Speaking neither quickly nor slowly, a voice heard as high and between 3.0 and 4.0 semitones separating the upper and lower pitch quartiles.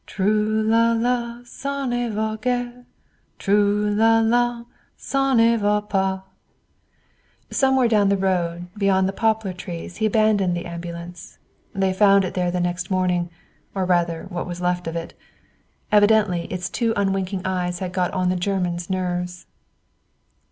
Yes: average, 150 wpm; high, 195 Hz; average, 3.6 semitones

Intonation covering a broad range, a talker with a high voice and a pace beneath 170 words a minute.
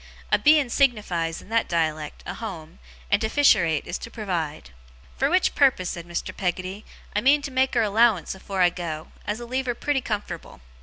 No: wide, 6.2 semitones; high, 210 Hz; average, 195 wpm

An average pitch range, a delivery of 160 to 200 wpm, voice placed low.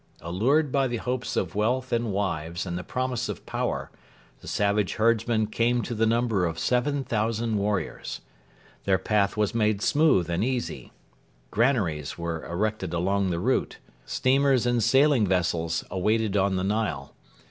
No: average, 4.6 semitones; average, 150 wpm; low, 105 Hz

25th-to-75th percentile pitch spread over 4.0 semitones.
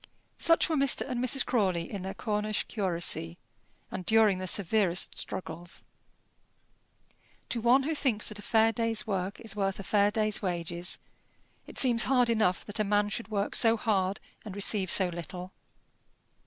No: average, 3.4 semitones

